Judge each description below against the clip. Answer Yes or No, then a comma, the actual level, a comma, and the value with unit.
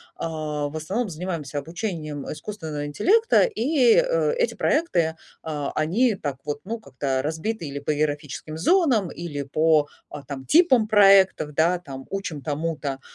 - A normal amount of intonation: No, wide, 6.5 semitones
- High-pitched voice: No, medium, 160 Hz